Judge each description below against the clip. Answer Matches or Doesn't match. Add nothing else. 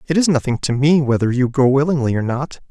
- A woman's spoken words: Doesn't match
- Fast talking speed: Matches